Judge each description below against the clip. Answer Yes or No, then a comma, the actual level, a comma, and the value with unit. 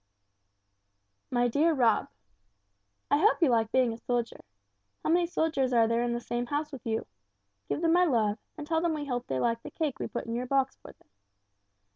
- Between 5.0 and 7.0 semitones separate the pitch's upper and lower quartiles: No, average, 4.6 semitones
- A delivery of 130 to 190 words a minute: No, fast, 205 wpm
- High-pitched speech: Yes, very high, 255 Hz